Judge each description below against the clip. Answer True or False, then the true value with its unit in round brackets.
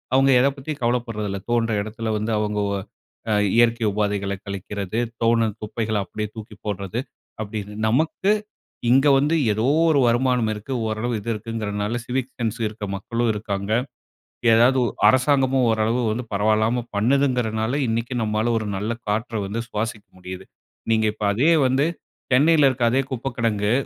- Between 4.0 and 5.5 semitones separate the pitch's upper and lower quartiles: False (2.7 semitones)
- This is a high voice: False (115 Hz)